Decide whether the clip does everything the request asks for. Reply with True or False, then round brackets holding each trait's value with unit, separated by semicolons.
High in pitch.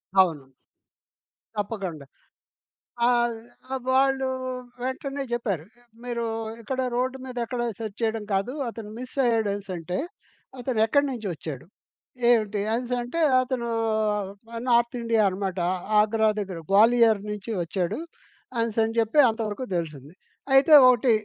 True (225 Hz)